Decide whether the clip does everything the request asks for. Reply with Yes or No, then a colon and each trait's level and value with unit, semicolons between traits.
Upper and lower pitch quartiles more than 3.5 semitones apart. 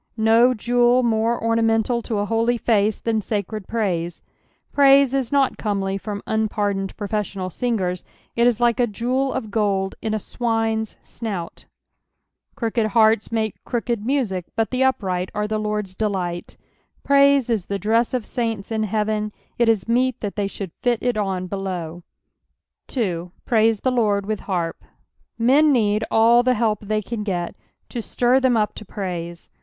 No: average, 3.0 semitones